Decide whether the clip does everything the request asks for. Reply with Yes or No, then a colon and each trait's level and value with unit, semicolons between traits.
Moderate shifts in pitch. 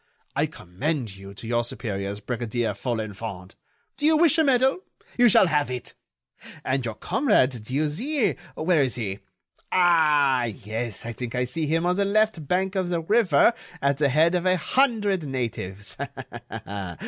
No: wide, 8.0 semitones